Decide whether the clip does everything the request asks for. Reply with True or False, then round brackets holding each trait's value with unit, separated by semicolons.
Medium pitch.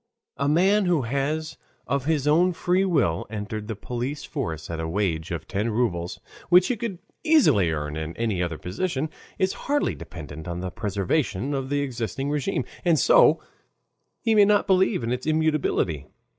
False (130 Hz)